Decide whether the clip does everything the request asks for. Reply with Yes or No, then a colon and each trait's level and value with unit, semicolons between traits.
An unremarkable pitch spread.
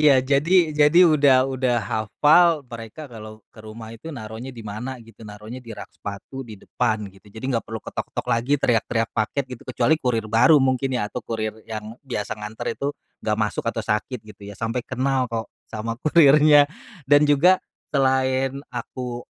Yes: average, 3.8 semitones